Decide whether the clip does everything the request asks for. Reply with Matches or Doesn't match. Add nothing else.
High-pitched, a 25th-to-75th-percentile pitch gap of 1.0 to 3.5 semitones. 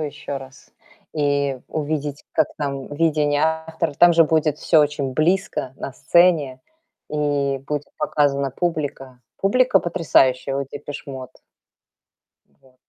Doesn't match